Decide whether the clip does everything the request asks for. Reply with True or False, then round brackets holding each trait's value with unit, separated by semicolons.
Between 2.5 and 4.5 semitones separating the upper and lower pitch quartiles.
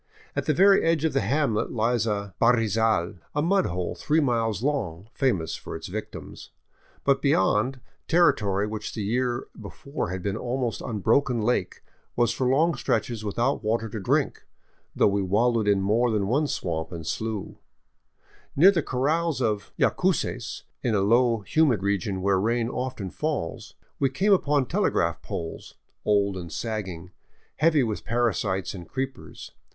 False (5.0 semitones)